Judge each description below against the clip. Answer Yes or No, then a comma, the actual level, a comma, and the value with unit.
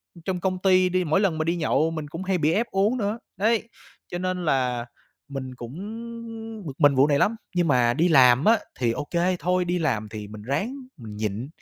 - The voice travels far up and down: Yes, wide, 6.2 semitones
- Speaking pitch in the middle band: Yes, medium, 160 Hz